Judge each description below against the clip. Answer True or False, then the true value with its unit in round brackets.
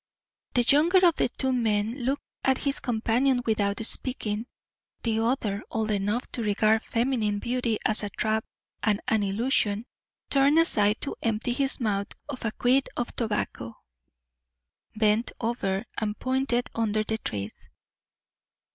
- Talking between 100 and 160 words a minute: True (140 wpm)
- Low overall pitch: False (225 Hz)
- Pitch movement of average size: True (3.3 semitones)